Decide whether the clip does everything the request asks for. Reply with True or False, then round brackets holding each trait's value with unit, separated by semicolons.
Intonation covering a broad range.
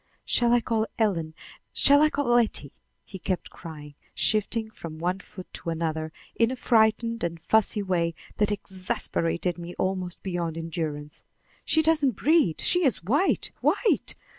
True (5.7 semitones)